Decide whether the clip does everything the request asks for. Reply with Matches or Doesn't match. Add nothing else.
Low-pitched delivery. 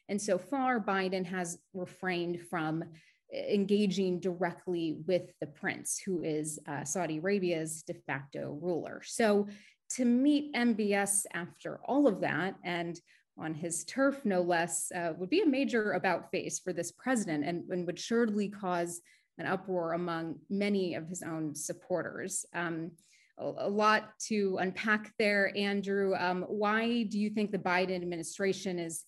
Doesn't match